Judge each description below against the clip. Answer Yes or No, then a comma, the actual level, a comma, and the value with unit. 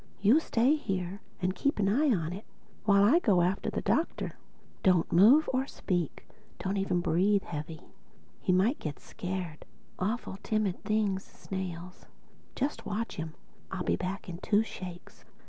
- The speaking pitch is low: No, high, 195 Hz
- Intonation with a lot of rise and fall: No, average, 3.3 semitones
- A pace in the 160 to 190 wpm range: No, average, 150 wpm